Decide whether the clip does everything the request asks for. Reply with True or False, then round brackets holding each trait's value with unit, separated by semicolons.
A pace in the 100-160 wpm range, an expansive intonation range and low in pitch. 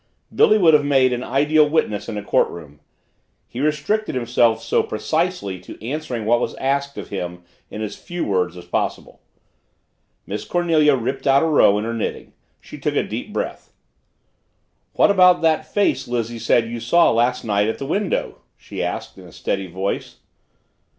False (175 wpm; 6.6 semitones; 125 Hz)